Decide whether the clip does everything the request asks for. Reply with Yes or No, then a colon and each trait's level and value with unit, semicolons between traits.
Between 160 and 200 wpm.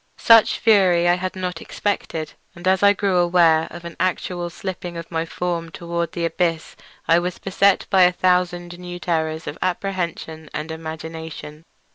Yes: average, 165 wpm